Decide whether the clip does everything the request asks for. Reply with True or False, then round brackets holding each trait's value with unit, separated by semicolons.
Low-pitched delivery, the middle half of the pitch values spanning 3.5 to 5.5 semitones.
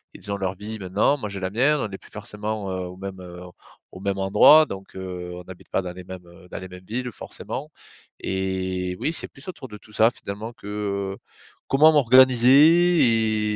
True (100 Hz; 4.1 semitones)